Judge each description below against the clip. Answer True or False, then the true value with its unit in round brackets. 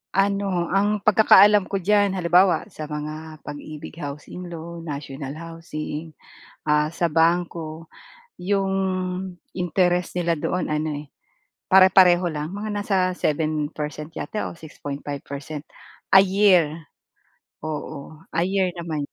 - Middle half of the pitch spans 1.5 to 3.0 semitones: False (3.6 semitones)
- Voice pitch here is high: False (165 Hz)